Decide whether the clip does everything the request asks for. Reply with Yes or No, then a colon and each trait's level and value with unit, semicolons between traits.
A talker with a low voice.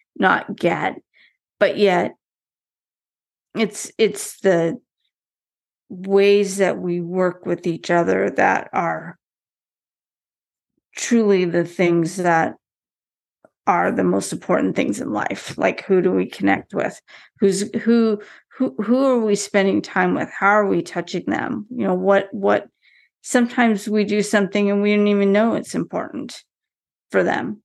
No: high, 200 Hz